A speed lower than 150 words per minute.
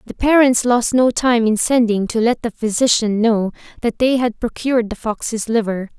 No: average, 190 wpm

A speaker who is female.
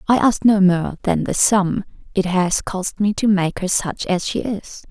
Yes: female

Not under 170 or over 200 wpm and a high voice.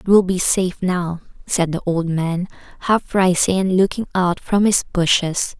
No: average, 180 wpm; medium, 180 Hz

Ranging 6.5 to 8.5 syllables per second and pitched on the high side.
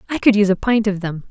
Yes: 7.6 syllables/s; high, 205 Hz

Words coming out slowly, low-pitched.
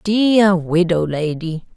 No: slow, 100 wpm; medium, 180 Hz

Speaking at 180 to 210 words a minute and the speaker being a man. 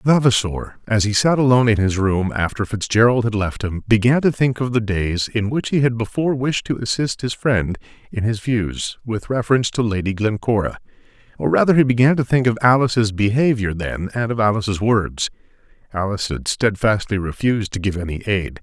Yes: average, 185 wpm; male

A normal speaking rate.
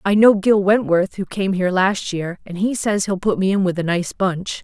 No: fast, 260 wpm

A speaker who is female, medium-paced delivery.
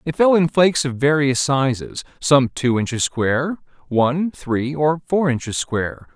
No: male; average, 165 wpm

